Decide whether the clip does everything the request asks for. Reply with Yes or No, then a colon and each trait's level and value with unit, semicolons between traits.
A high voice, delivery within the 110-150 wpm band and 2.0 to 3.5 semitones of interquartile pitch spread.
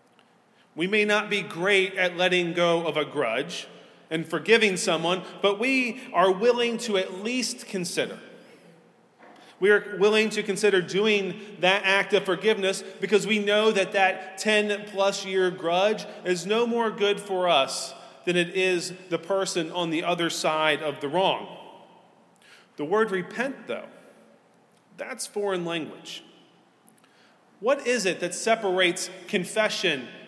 Yes: high, 195 Hz; average, 145 wpm; average, 2.9 semitones